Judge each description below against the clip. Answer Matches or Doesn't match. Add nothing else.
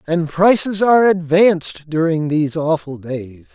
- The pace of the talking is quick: Doesn't match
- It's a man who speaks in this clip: Matches